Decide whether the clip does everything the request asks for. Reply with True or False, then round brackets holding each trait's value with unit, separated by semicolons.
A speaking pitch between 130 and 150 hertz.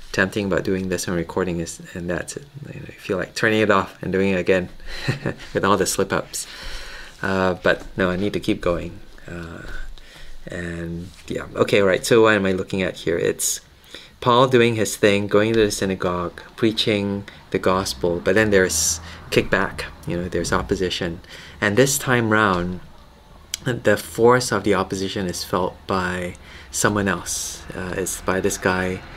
False (95 Hz)